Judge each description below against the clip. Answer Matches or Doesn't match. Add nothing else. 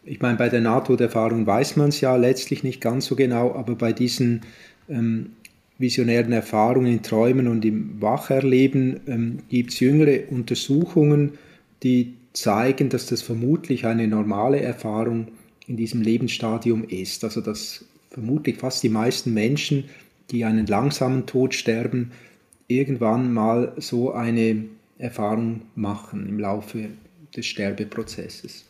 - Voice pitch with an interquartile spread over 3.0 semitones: Doesn't match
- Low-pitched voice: Matches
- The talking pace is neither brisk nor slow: Matches